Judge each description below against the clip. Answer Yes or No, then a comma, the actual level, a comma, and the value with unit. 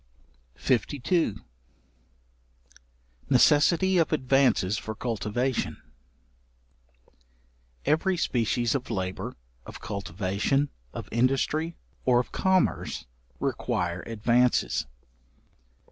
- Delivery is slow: Yes, slow, 70 wpm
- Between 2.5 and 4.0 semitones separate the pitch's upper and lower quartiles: No, average, 5.3 semitones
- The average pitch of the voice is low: Yes, low, 125 Hz